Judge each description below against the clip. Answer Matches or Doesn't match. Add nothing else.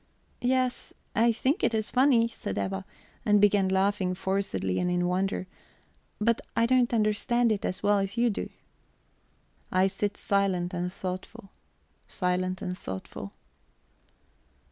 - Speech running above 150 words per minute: Doesn't match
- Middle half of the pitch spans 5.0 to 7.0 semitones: Doesn't match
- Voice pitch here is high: Matches